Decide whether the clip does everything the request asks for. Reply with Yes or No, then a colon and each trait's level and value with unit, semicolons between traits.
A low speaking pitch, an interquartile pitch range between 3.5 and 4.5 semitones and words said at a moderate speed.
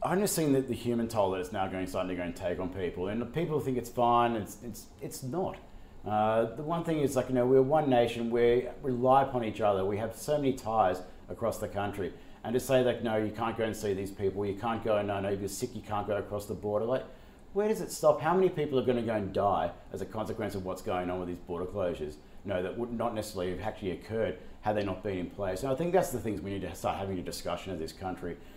No: low, 110 Hz; average, 4.2 semitones; fast, 280 wpm